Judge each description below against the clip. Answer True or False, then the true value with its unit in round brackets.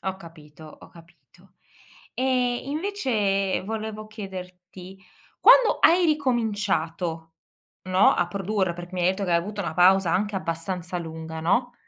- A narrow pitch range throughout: False (3.7 semitones)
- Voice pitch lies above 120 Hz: True (190 Hz)